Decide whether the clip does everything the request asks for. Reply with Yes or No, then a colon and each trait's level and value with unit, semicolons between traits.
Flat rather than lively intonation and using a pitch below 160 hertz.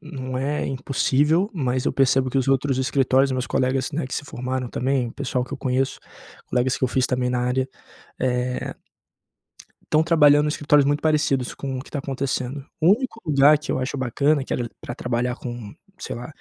Yes: narrow, 2.3 semitones; low, 135 Hz